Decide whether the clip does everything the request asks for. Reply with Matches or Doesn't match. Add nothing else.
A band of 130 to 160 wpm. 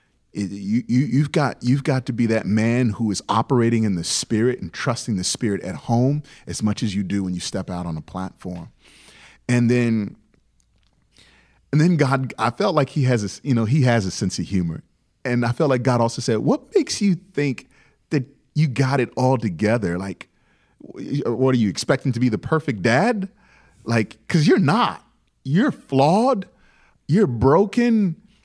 Doesn't match